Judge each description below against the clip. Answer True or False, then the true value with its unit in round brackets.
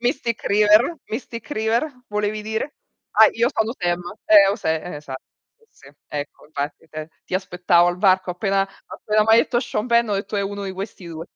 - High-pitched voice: True (205 Hz)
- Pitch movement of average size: True (3.8 semitones)